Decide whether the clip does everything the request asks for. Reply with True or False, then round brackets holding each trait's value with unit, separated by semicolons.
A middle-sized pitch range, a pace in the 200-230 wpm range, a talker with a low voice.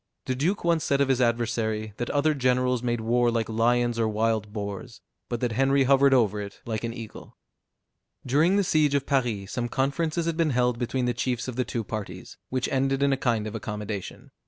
True (3.4 semitones; 205 wpm; 120 Hz)